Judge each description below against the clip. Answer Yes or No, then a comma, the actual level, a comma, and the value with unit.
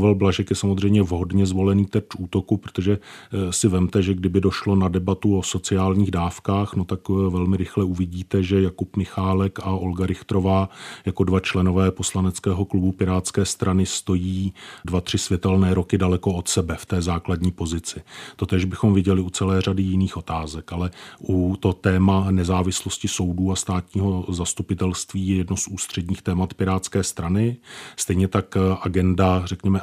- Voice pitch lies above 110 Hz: No, very low, 95 Hz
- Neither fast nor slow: Yes, average, 155 wpm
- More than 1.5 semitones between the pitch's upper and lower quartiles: No, narrow, 1.0 semitones